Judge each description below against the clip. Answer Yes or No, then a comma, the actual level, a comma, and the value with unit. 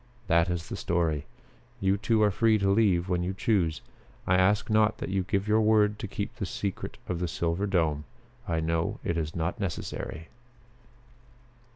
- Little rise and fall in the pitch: No, average, 3.8 semitones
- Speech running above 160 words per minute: Yes, average, 175 wpm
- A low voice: Yes, very low, 95 Hz